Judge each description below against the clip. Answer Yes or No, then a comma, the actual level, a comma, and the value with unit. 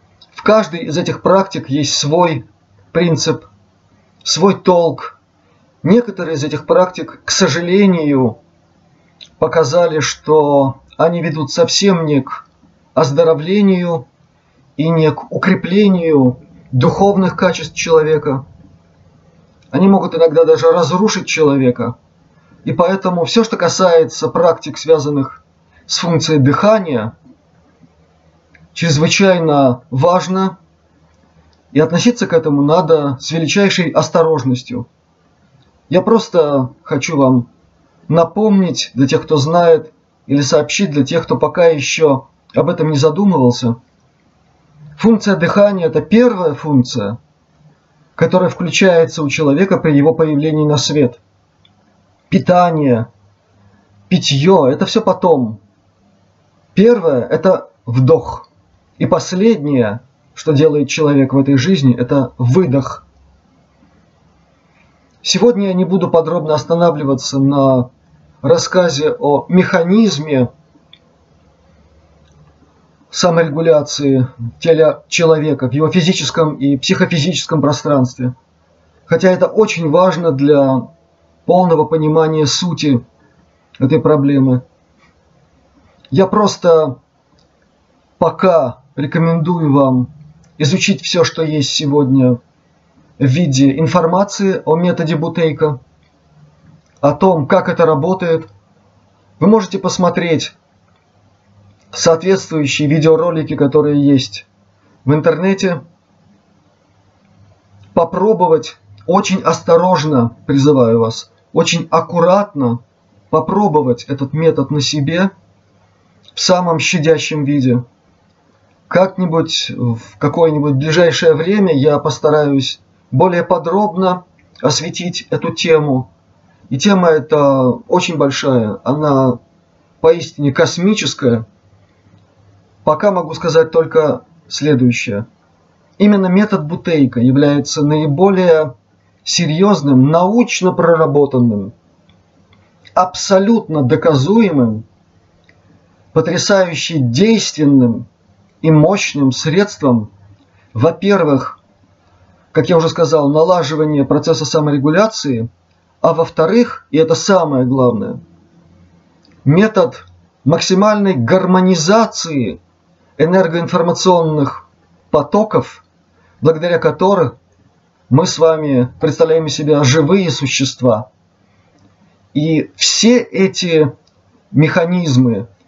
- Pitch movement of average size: No, wide, 5.7 semitones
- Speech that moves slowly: Yes, slow, 90 wpm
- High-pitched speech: No, medium, 155 Hz